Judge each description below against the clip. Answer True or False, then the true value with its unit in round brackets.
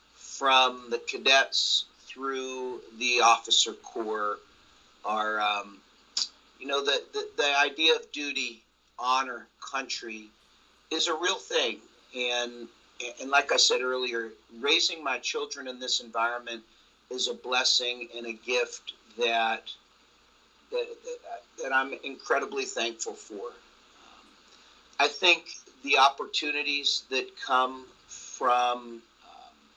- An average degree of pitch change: False (5.7 semitones)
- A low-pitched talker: True (130 Hz)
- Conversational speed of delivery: False (115 wpm)